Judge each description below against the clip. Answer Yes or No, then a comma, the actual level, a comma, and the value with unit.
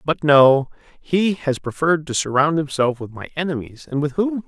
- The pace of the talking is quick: No, average, 190 wpm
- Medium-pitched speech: Yes, medium, 145 Hz